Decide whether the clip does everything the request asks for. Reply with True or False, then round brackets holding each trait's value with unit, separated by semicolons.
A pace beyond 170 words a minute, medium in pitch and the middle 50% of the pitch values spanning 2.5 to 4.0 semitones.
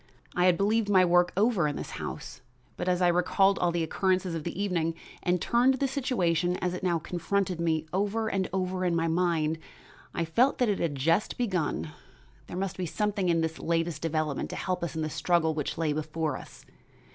True (205 wpm; 175 Hz; 3.0 semitones)